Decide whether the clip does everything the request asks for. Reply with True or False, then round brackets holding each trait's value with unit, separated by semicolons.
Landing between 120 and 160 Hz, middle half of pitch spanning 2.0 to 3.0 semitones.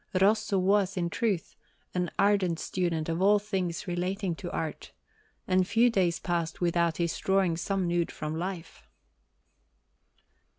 False (180 Hz; 2.4 semitones)